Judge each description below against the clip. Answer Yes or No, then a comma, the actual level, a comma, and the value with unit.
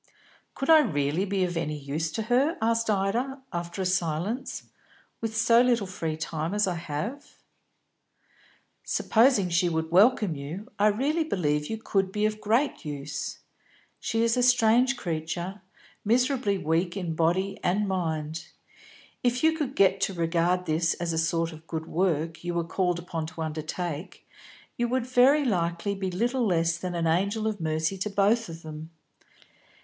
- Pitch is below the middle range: No, medium, 185 Hz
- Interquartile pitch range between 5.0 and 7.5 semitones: Yes, wide, 5.5 semitones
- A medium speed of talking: Yes, average, 165 wpm